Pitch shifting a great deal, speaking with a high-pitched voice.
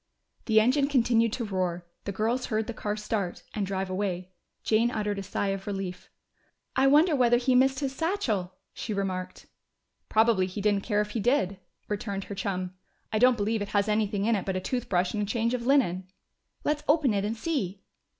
No: average, 3.7 semitones; high, 210 Hz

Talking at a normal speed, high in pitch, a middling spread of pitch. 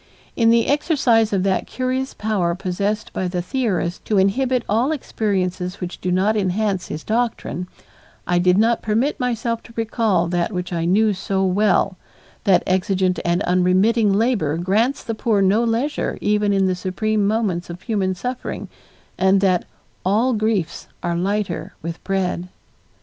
Yes: average, 155 wpm; high, 200 Hz; average, 3.7 semitones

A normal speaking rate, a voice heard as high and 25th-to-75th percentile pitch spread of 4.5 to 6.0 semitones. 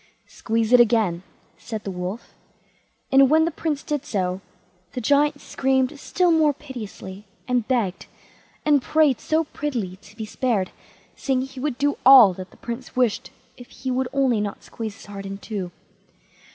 Yes: average, 165 wpm; high, 245 Hz; average, 5.1 semitones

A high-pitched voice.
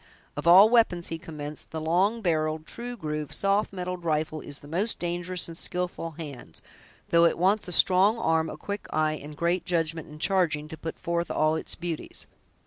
No: medium, 170 Hz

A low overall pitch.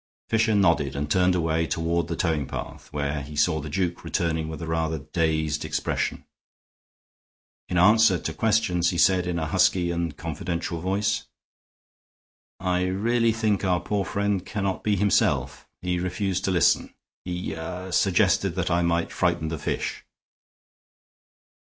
Yes: very low, 90 Hz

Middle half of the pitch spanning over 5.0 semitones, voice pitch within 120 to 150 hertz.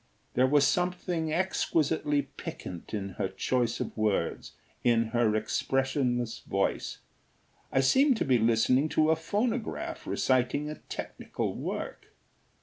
Yes: wide, 5.5 semitones; low, 135 Hz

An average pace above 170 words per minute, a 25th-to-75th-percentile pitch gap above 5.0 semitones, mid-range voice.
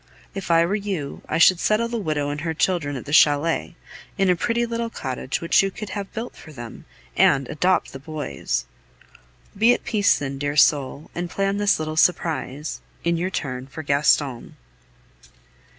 Yes: average, 180 wpm; wide, 5.4 semitones; medium, 165 Hz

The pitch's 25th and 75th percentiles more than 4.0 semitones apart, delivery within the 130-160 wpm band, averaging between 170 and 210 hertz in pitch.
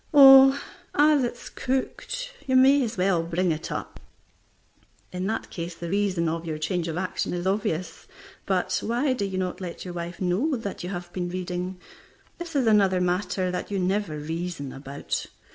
No: average, 4.5 semitones; average, 180 wpm; medium, 185 Hz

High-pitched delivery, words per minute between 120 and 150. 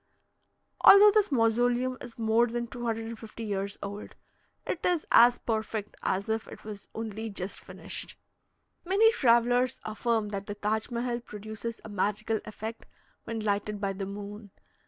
Yes: high, 225 Hz; average, 145 wpm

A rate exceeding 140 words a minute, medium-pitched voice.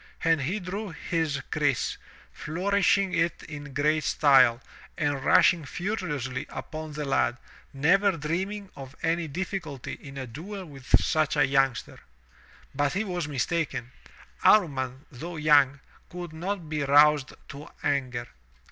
No: slow, 135 wpm; medium, 150 Hz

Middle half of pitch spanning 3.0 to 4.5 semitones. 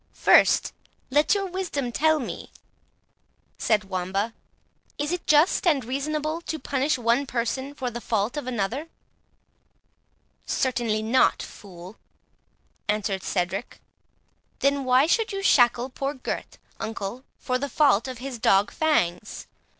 No: average, 5.2 semitones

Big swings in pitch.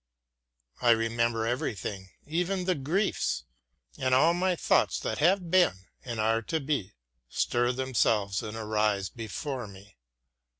Yes: wide, 6.5 semitones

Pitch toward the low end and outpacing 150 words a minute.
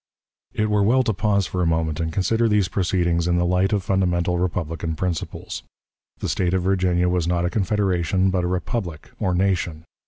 Yes: very low, 90 Hz; average, 190 wpm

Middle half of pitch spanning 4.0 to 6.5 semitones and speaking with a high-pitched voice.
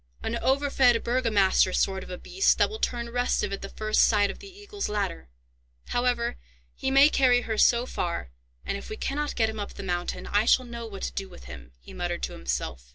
Yes: average, 4.8 semitones; high, 225 Hz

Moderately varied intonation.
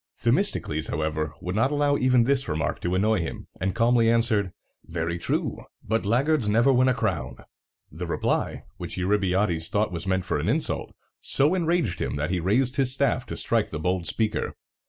No: wide, 6.4 semitones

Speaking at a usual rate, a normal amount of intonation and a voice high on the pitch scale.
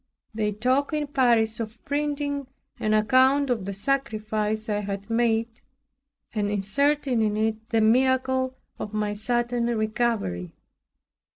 No: slow, 125 wpm; average, 3.4 semitones; high, 225 Hz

